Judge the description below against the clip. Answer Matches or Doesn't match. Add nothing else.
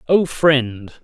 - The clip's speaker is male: Matches